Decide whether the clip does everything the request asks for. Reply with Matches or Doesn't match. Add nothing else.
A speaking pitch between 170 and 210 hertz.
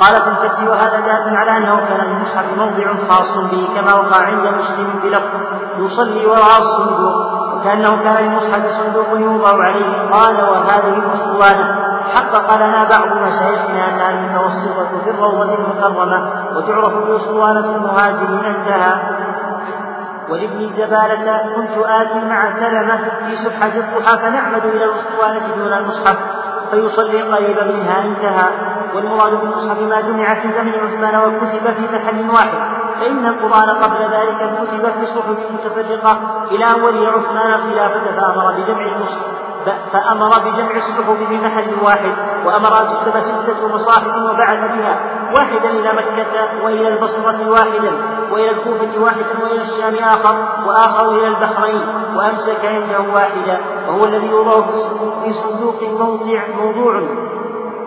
Doesn't match